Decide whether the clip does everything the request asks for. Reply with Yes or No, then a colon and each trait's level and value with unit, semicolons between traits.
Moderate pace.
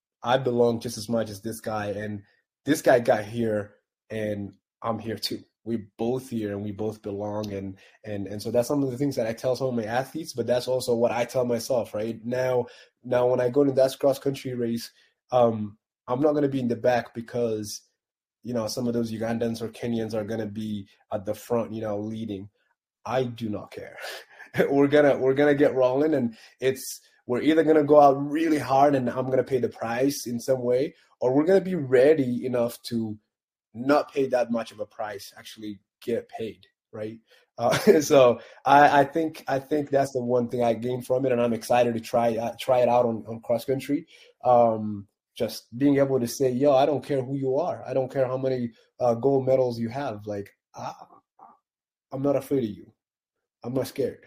No: fast, 220 wpm